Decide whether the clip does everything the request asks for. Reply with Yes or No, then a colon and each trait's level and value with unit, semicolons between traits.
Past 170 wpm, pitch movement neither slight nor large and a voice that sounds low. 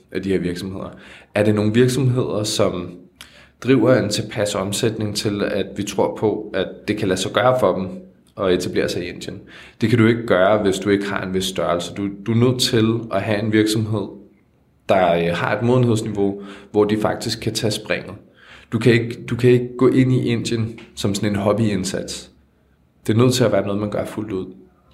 Yes: average, 205 wpm; average, 3.5 semitones; low, 105 Hz